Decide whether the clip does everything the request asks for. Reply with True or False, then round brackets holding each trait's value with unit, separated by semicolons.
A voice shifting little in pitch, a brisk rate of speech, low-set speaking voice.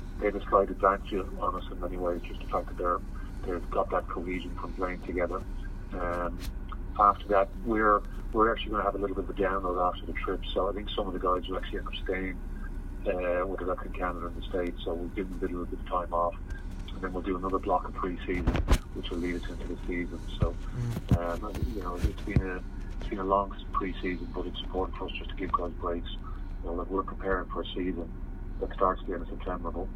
True (1.6 semitones; 245 wpm; 90 Hz)